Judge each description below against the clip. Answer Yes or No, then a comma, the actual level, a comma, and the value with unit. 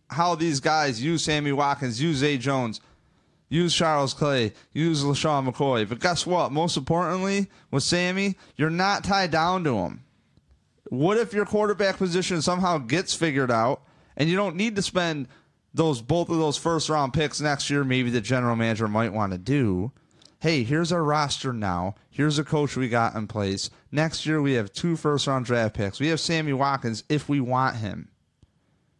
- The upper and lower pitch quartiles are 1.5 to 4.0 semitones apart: No, average, 4.7 semitones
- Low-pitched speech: No, medium, 150 Hz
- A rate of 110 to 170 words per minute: No, average, 185 wpm